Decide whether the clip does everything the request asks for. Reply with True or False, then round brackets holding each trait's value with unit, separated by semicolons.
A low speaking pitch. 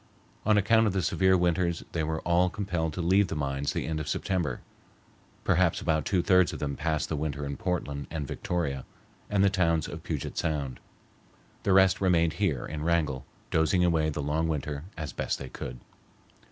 True (80 Hz)